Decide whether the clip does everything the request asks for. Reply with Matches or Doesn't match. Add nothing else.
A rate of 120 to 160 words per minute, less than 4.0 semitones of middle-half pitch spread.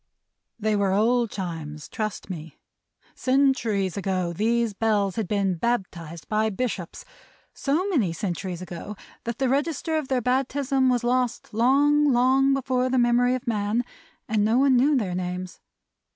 Doesn't match